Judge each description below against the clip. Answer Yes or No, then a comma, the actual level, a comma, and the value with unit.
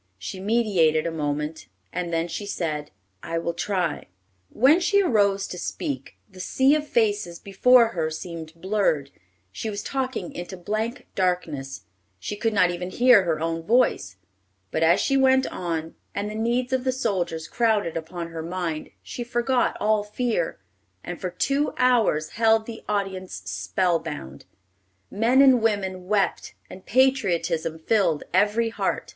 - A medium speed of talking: Yes, average, 155 wpm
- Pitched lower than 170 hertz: No, high, 190 Hz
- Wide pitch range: Yes, wide, 5.7 semitones